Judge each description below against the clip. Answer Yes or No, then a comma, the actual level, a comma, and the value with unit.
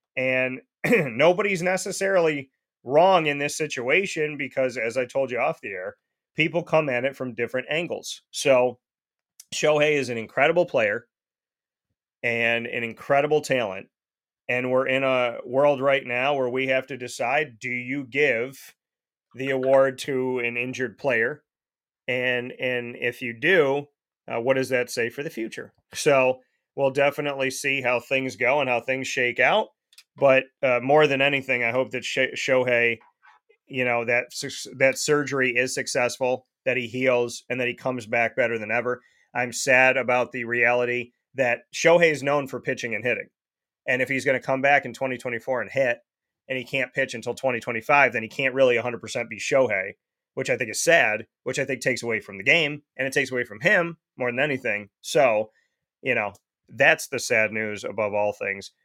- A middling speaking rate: Yes, average, 180 wpm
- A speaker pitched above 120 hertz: Yes, low, 130 Hz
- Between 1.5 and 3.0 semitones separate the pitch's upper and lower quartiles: Yes, narrow, 2.5 semitones